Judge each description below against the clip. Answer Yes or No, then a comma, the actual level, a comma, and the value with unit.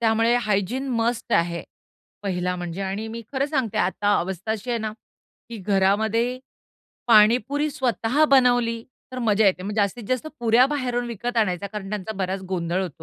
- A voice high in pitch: Yes, high, 220 Hz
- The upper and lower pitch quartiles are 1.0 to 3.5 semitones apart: No, average, 3.9 semitones